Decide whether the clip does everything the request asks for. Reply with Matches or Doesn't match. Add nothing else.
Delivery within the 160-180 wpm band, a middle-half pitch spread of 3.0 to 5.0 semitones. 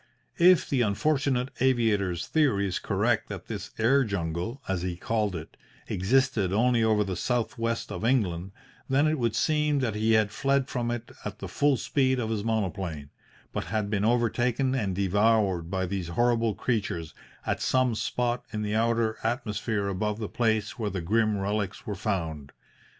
Matches